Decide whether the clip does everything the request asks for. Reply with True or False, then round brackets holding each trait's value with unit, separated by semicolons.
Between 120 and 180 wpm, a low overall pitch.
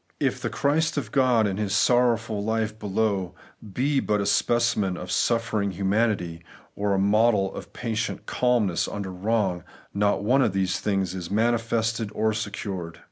True (160 wpm; 105 Hz)